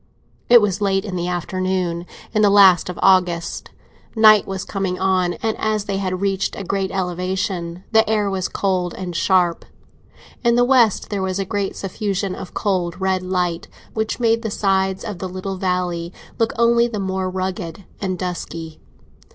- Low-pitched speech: No, high, 190 Hz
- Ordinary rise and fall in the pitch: No, narrow, 2.0 semitones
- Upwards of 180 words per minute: No, average, 175 wpm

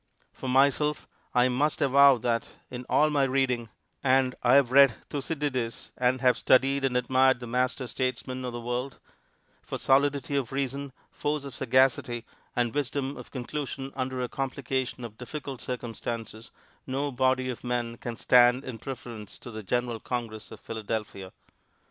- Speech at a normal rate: Yes, average, 155 wpm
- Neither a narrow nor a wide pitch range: No, narrow, 2.1 semitones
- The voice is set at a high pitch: No, low, 130 Hz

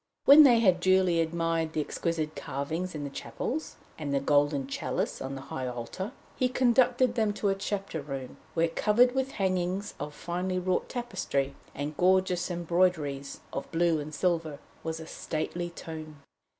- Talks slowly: No, average, 165 wpm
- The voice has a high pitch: No, medium, 170 Hz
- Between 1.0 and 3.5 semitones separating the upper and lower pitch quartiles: No, average, 4.2 semitones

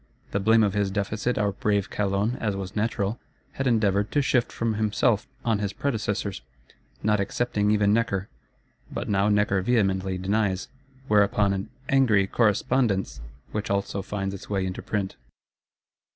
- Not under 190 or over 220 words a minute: No, average, 150 wpm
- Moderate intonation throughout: No, narrow, 1.9 semitones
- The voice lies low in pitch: Yes, low, 105 Hz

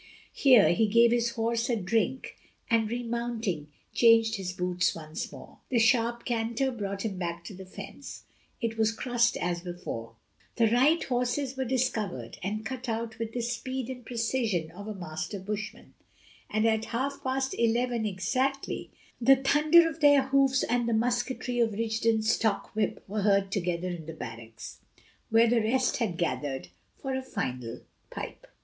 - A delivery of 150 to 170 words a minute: Yes, average, 165 wpm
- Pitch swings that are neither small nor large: Yes, average, 4.1 semitones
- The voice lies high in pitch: Yes, high, 225 Hz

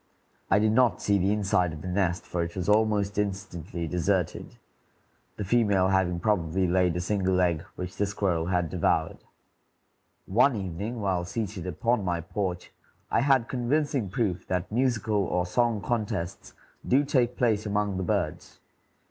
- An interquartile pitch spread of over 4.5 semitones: No, average, 3.5 semitones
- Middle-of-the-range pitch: No, very low, 95 Hz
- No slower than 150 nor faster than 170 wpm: Yes, average, 155 wpm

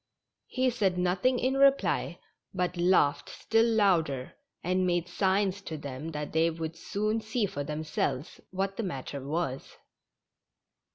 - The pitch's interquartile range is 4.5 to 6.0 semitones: Yes, average, 4.8 semitones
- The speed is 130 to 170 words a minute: Yes, average, 145 wpm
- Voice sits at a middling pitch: Yes, medium, 180 Hz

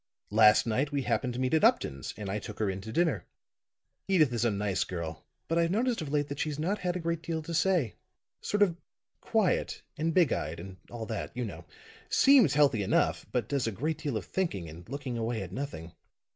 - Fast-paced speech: Yes, fast, 220 wpm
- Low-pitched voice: Yes, low, 130 Hz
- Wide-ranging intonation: Yes, wide, 7.5 semitones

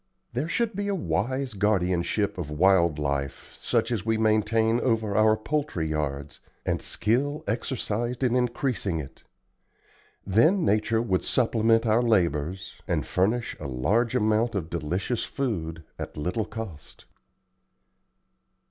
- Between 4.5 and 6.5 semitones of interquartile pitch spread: Yes, average, 5.2 semitones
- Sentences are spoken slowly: Yes, slow, 130 wpm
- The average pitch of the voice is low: Yes, low, 110 Hz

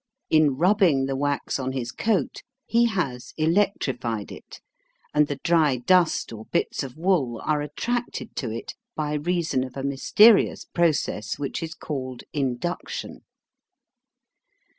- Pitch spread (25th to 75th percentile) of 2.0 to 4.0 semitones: No, average, 4.9 semitones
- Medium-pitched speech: Yes, medium, 150 Hz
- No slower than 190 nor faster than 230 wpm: No, slow, 135 wpm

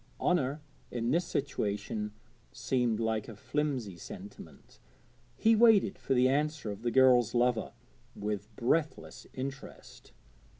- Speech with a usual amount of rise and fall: Yes, average, 5.0 semitones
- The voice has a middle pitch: No, low, 125 Hz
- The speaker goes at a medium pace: No, slow, 120 wpm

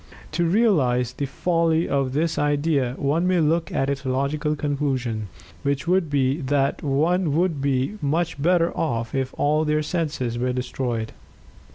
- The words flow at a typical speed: Yes, average, 160 wpm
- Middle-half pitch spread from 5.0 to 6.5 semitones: No, average, 3.7 semitones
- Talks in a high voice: No, medium, 145 Hz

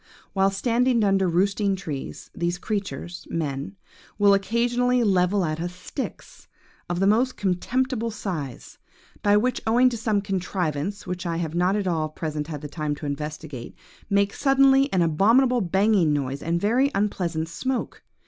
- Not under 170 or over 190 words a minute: No, average, 160 wpm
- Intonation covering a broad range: No, average, 5.0 semitones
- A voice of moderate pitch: No, high, 195 Hz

